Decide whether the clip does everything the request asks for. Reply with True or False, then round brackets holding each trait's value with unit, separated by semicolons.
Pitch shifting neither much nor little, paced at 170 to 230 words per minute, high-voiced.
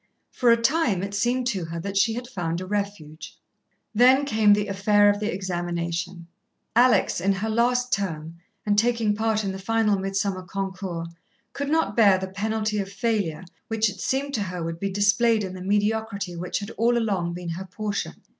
True (3.1 semitones; 190 wpm; 200 Hz)